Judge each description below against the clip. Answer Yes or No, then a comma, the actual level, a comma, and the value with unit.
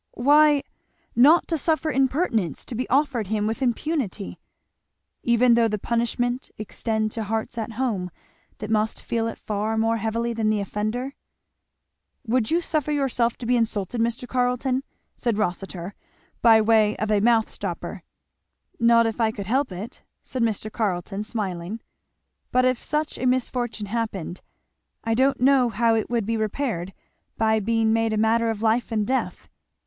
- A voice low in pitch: No, high, 230 Hz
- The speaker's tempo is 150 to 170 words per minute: Yes, average, 160 wpm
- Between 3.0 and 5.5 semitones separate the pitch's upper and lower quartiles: No, narrow, 2.6 semitones